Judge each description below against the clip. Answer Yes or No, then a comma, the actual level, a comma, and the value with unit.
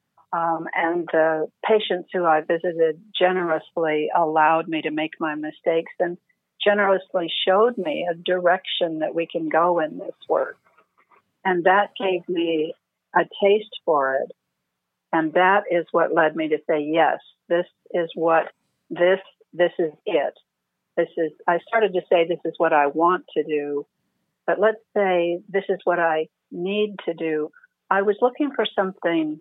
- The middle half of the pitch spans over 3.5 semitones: No, average, 2.8 semitones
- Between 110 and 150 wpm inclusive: No, average, 160 wpm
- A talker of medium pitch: Yes, medium, 170 Hz